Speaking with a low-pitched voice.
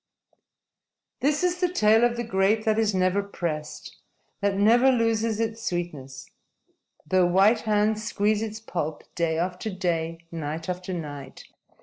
No: high, 200 Hz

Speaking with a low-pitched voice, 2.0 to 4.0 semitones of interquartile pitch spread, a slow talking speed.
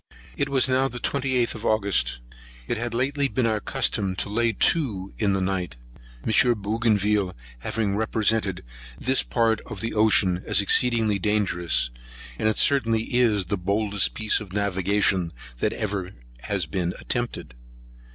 No: low, 105 Hz; average, 3.3 semitones; average, 150 wpm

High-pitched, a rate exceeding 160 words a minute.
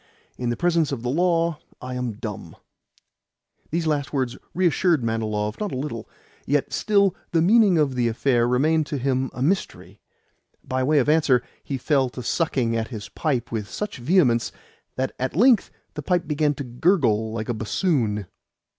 No: low, 135 Hz; average, 170 wpm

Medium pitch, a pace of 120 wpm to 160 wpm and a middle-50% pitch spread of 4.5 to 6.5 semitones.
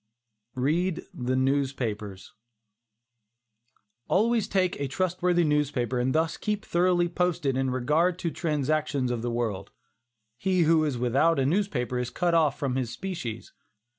Yes: medium, 150 Hz; average, 140 wpm; wide, 5.6 semitones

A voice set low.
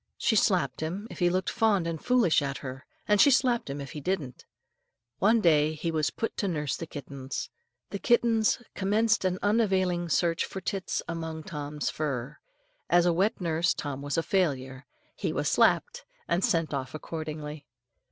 No: medium, 165 Hz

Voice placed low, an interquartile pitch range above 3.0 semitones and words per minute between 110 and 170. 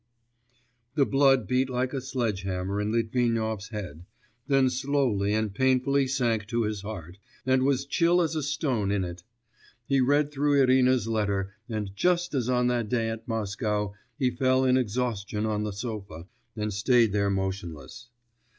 Yes: low, 115 Hz; average, 4.2 semitones; average, 160 wpm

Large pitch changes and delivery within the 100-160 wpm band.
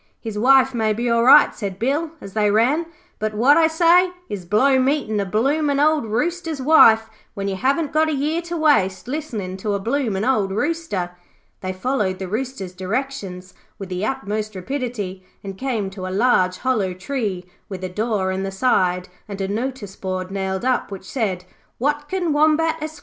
No: wide, 6.5 semitones; average, 180 wpm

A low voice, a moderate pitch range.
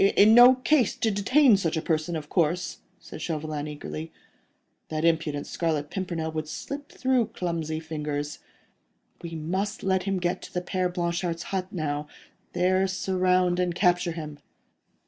No: medium, 175 Hz; average, 3.3 semitones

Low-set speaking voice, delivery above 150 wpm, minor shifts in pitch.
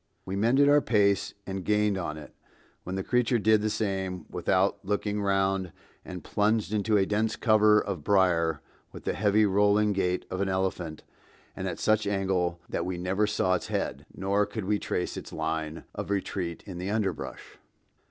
Yes: low, 100 Hz; average, 180 wpm; narrow, 2.3 semitones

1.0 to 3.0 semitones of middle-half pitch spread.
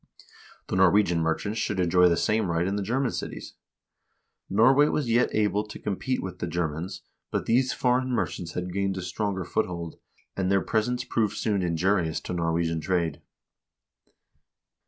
No: average, 3.8 semitones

